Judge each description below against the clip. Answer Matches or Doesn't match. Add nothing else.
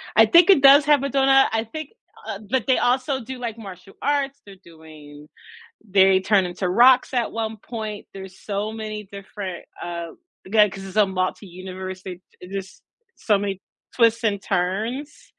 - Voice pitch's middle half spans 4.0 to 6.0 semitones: Matches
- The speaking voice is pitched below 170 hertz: Doesn't match